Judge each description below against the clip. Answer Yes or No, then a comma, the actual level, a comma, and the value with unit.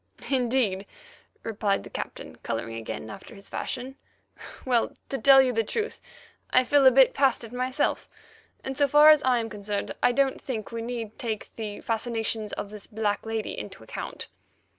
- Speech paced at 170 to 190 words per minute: Yes, average, 175 wpm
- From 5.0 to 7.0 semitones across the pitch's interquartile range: No, average, 3.7 semitones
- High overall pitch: Yes, high, 230 Hz